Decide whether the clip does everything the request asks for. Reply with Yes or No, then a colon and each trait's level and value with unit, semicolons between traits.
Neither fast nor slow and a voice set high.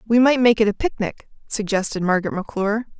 Yes: average, 180 wpm; high, 215 Hz